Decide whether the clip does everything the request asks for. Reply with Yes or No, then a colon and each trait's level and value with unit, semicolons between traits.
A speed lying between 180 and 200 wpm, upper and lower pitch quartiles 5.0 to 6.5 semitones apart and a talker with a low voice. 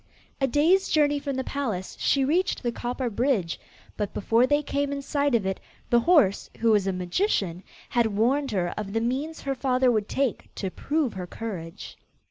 No: average, 190 wpm; wide, 5.6 semitones; high, 245 Hz